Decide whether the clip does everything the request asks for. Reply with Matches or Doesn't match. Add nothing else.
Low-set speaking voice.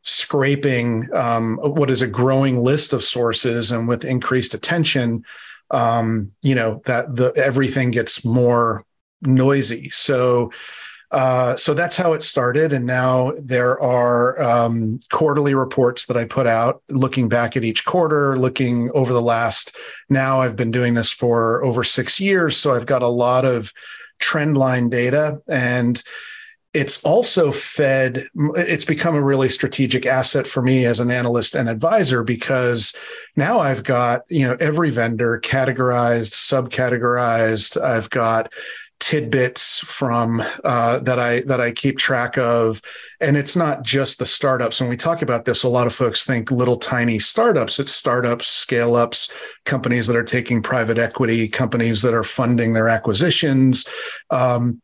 Matches